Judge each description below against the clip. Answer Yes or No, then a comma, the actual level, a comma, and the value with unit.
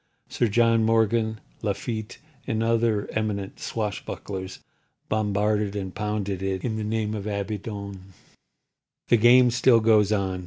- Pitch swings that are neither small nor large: No, narrow, 2.0 semitones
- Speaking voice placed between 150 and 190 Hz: No, low, 105 Hz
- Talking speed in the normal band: No, slow, 130 wpm